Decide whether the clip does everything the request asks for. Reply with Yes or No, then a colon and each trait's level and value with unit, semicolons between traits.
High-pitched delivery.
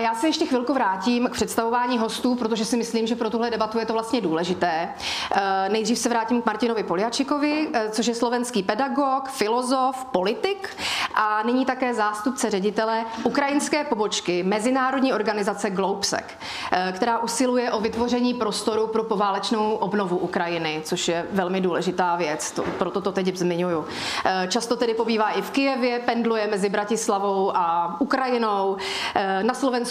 Yes: high, 225 Hz